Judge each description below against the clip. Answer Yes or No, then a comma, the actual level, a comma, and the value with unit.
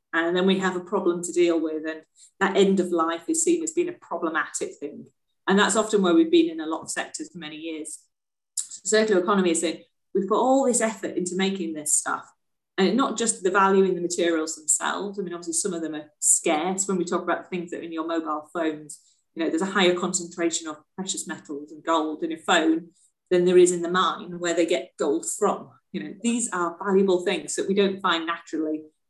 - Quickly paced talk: Yes, fast, 235 wpm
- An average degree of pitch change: Yes, average, 3.4 semitones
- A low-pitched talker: No, medium, 180 Hz